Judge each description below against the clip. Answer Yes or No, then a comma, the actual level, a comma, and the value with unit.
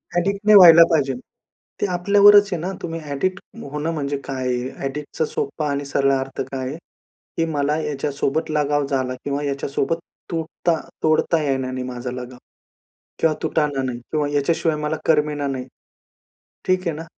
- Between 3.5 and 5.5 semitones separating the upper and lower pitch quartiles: No, average, 3.0 semitones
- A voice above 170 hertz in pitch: No, medium, 150 Hz